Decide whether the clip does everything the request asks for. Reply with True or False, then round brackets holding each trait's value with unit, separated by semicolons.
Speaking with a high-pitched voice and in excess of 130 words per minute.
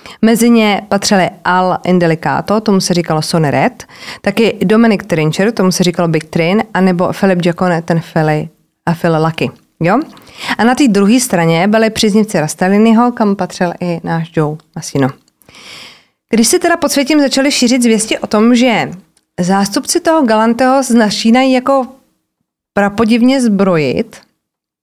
True (200 Hz; 145 wpm)